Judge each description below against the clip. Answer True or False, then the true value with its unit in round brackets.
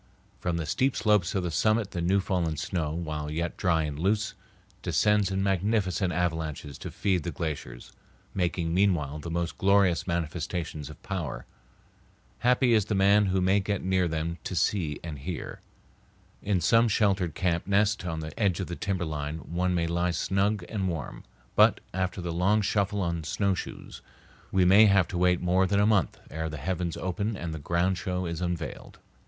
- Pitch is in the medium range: False (90 Hz)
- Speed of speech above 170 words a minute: True (180 wpm)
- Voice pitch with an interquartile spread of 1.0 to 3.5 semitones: True (3.1 semitones)